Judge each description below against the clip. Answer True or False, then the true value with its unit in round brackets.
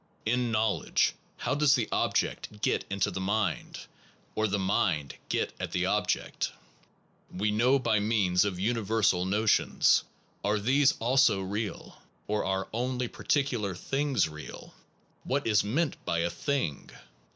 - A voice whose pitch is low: True (110 Hz)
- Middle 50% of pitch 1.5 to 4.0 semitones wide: False (4.6 semitones)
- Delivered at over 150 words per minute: False (140 wpm)